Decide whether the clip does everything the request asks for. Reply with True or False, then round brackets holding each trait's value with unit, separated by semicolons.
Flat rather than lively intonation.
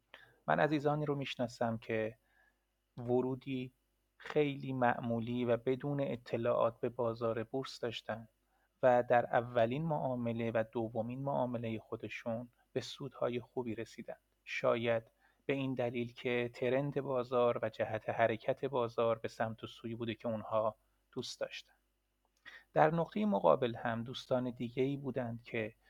True (2.3 semitones)